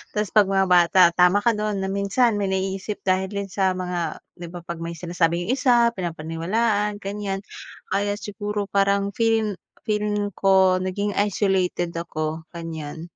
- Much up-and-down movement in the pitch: No, average, 2.8 semitones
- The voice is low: No, high, 195 Hz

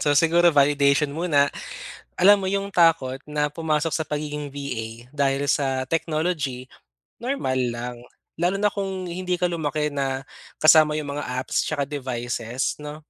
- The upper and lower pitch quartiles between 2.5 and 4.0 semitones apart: Yes, average, 3.3 semitones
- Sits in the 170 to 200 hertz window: No, medium, 150 Hz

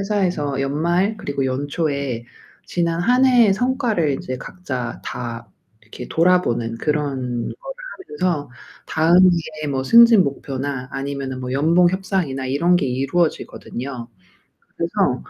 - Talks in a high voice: No, medium, 150 Hz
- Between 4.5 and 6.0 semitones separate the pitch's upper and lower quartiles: Yes, wide, 5.6 semitones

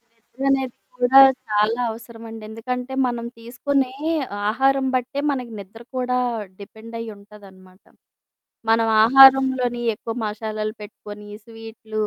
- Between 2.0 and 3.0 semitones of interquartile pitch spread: Yes, average, 2.7 semitones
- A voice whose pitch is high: Yes, high, 230 Hz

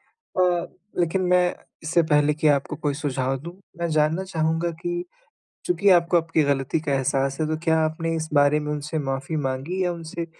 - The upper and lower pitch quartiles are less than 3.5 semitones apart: Yes, average, 2.9 semitones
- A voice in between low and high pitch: Yes, medium, 160 Hz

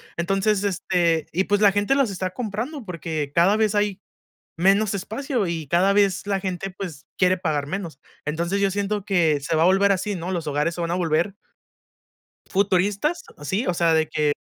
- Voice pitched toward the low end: No, high, 190 Hz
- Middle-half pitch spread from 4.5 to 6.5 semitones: No, average, 3.3 semitones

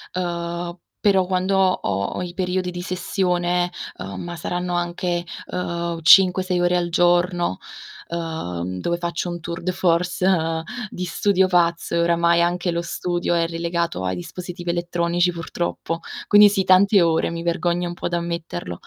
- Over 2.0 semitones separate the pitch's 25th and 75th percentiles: No, narrow, 1.0 semitones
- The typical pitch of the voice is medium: Yes, medium, 175 Hz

